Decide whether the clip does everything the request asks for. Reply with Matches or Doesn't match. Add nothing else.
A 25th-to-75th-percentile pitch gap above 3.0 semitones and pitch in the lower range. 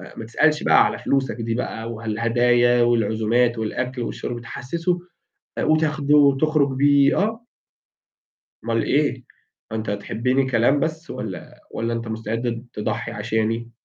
Matches